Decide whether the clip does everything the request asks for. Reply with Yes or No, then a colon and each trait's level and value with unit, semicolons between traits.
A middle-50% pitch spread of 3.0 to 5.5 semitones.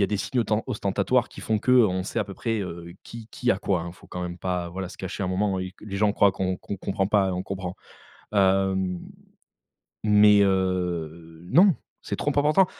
No: narrow, 2.5 semitones